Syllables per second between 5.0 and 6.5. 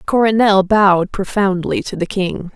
No: 4.5 syllables/s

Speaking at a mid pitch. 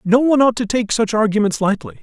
No: high, 225 Hz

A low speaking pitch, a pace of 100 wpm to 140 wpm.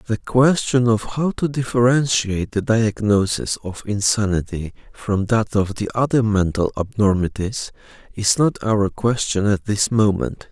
Yes: low, 110 Hz; slow, 135 wpm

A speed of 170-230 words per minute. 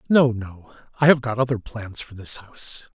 Yes: fast, 205 wpm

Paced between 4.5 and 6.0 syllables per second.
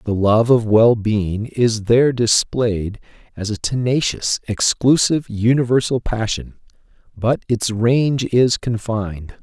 No: 4.0 syllables/s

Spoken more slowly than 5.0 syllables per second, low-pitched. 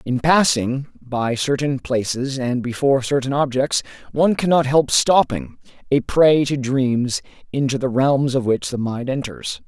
Yes: 4.3 syllables/s; low, 130 Hz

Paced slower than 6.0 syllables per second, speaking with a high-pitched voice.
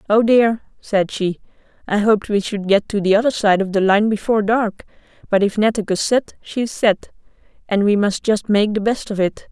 Yes: 5.2 syllables/s; high, 210 Hz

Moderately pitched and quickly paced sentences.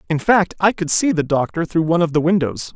Yes: medium, 170 Hz; fast, 260 wpm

